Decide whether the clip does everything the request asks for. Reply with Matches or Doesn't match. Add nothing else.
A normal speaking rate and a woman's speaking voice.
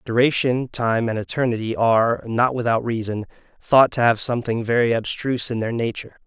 Doesn't match